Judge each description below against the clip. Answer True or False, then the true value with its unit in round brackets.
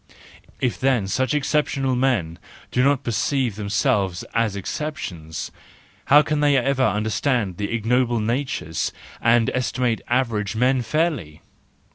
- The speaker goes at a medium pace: False (120 wpm)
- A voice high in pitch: False (120 Hz)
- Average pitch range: True (4.4 semitones)